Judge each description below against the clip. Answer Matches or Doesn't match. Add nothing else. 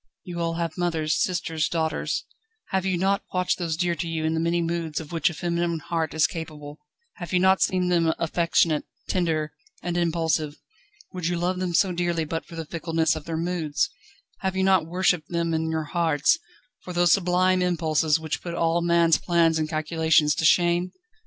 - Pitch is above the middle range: Doesn't match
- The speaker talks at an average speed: Matches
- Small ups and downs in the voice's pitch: Matches